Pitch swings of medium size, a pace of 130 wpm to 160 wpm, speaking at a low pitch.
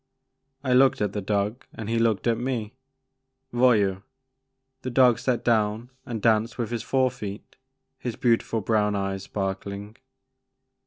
Yes: average, 3.1 semitones; average, 150 wpm; low, 115 Hz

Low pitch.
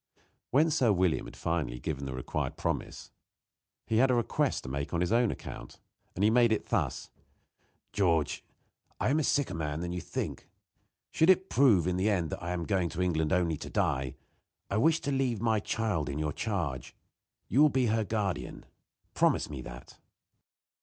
Yes: very low, 95 Hz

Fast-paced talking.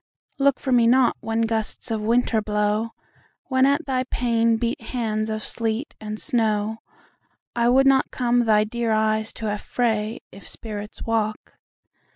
No: average, 140 wpm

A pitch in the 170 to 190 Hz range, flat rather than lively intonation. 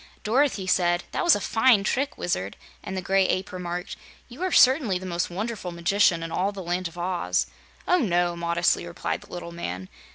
No: medium, 185 Hz; average, 3.3 semitones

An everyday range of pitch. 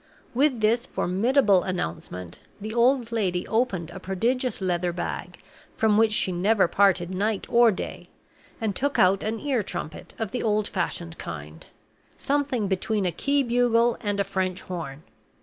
Yes: average, 4.4 semitones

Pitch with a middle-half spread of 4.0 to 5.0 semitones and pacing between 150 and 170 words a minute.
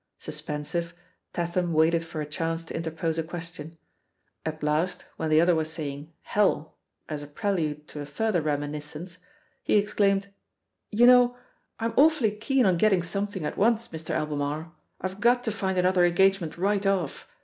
Yes: average, 4.4 semitones; average, 160 wpm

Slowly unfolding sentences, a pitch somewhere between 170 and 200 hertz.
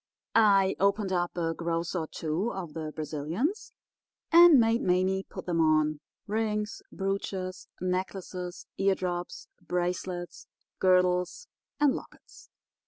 Yes: slow, 105 wpm; medium, 185 Hz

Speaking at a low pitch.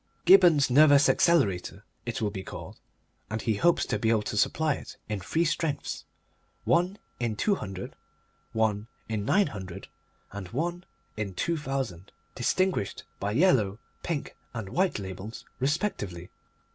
Yes: low, 115 Hz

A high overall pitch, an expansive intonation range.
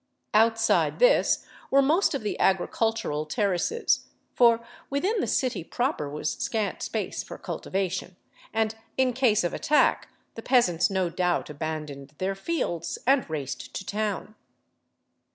Yes: high, 210 Hz; wide, 6.4 semitones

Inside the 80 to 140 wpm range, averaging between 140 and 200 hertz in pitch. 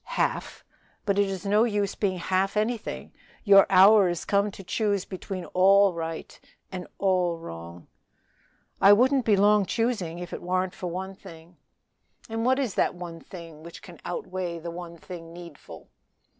No: average, 165 wpm; high, 190 Hz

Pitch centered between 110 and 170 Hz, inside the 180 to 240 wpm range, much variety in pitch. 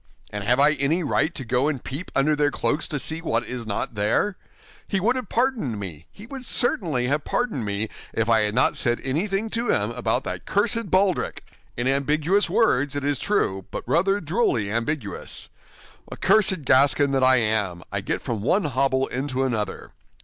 Yes: medium, 140 Hz; average, 185 wpm; wide, 7.6 semitones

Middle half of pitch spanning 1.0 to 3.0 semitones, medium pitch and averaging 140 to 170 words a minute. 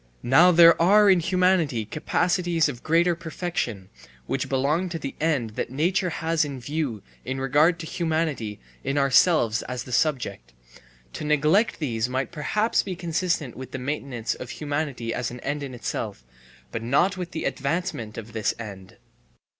No: wide, 5.5 semitones; medium, 145 Hz; average, 160 wpm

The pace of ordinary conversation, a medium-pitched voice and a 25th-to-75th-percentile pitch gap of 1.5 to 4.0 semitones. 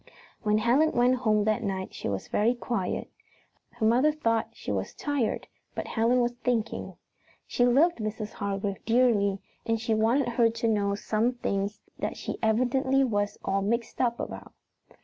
No: average, 165 wpm; high, 230 Hz; average, 2.7 semitones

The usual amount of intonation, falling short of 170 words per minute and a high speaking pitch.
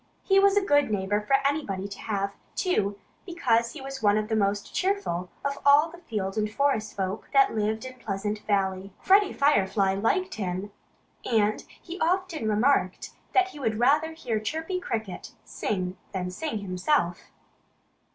No: wide, 7.1 semitones; average, 160 wpm; high, 220 Hz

